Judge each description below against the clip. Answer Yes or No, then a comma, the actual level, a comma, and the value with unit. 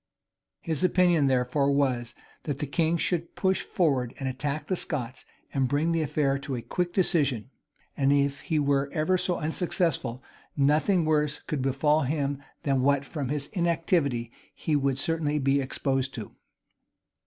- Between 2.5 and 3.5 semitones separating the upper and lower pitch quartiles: Yes, average, 3.0 semitones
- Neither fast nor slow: Yes, average, 155 wpm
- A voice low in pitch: No, medium, 145 Hz